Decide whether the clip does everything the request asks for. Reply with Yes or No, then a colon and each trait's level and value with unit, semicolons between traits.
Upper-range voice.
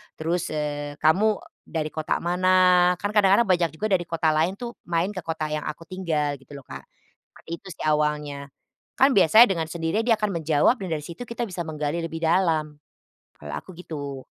No: medium, 165 Hz